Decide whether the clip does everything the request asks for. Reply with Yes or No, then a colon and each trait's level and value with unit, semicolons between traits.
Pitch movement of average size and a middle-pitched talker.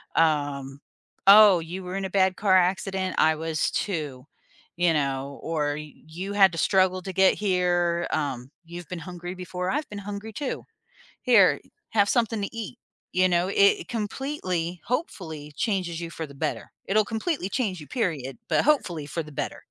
Yes: average, 4.0 semitones; medium, 180 Hz